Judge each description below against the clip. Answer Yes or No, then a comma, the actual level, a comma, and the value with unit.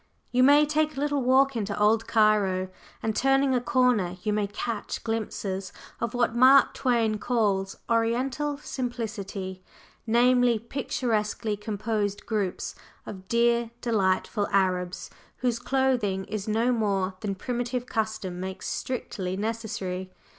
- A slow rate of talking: Yes, slow, 125 wpm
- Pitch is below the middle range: No, high, 225 Hz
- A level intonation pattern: No, average, 3.7 semitones